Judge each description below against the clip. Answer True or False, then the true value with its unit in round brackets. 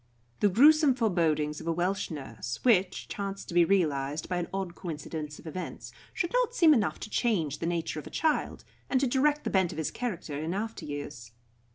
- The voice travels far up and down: True (6.8 semitones)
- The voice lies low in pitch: False (180 Hz)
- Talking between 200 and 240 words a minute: True (205 wpm)